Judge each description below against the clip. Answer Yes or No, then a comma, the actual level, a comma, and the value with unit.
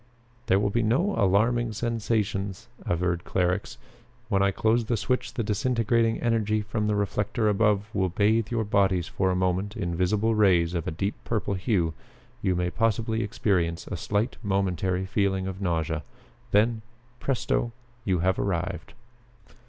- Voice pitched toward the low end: Yes, low, 100 Hz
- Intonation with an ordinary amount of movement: Yes, average, 3.3 semitones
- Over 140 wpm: Yes, average, 150 wpm